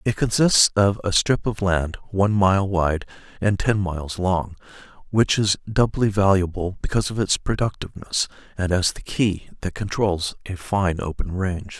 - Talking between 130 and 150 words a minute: No, average, 165 wpm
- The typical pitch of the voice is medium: No, very low, 95 Hz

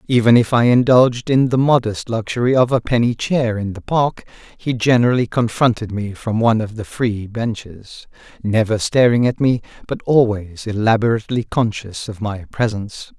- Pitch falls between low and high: No, low, 115 Hz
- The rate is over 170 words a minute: No, average, 165 wpm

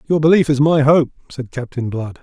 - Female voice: No, male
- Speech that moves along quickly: Yes, fast, 215 wpm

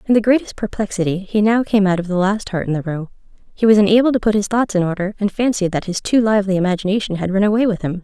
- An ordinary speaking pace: No, fast, 270 wpm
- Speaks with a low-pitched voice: No, high, 200 Hz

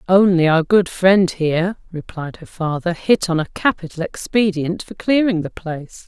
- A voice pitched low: No, medium, 180 Hz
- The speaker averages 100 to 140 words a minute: No, average, 170 wpm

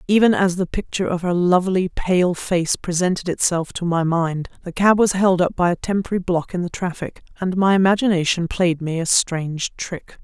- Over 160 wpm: Yes, average, 195 wpm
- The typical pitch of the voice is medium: Yes, medium, 180 Hz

